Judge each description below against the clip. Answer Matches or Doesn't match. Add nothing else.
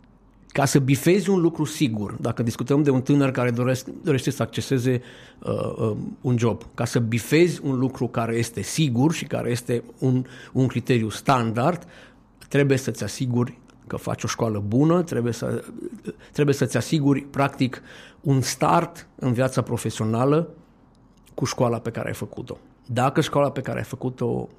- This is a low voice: Matches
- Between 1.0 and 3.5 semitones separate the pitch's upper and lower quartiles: Matches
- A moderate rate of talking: Matches